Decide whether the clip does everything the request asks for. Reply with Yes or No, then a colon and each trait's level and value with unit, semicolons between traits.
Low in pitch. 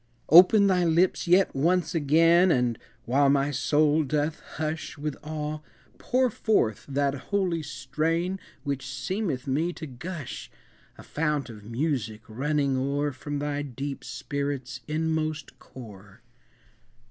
No: medium, 145 Hz